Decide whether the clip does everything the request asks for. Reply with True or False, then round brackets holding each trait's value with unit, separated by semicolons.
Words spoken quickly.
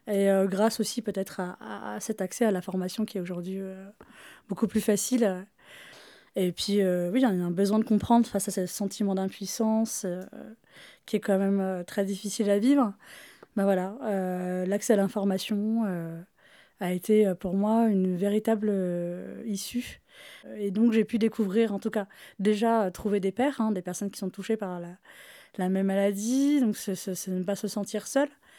False (195 wpm)